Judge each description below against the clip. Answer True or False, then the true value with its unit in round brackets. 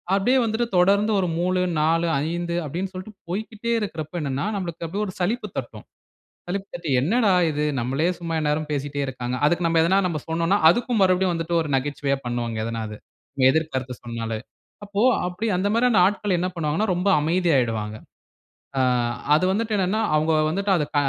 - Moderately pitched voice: True (170 Hz)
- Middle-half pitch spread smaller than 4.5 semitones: False (5.2 semitones)